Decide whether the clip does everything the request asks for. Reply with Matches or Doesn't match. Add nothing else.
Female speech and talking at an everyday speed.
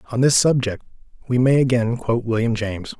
Doesn't match